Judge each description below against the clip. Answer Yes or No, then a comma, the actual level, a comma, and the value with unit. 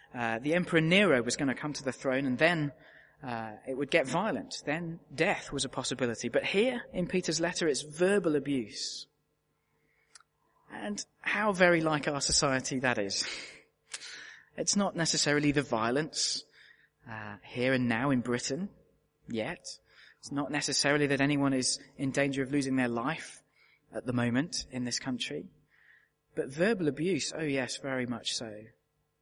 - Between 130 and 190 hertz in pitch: Yes, medium, 140 Hz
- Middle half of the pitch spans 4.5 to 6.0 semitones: No, average, 3.9 semitones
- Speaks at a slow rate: No, average, 160 wpm